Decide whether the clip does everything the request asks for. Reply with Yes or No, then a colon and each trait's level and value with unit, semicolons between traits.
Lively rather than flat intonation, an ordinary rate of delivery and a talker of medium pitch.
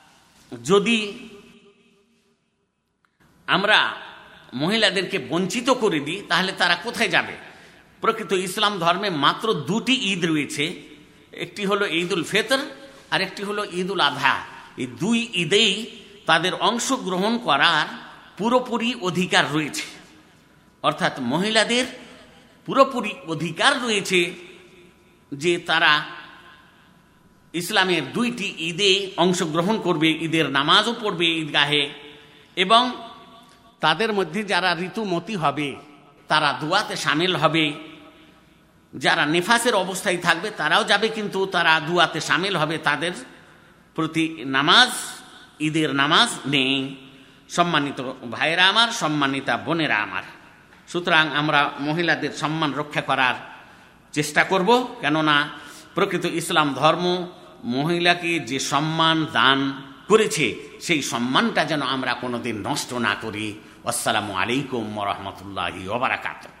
Yes: wide, 5.7 semitones; average, 100 wpm; medium, 170 Hz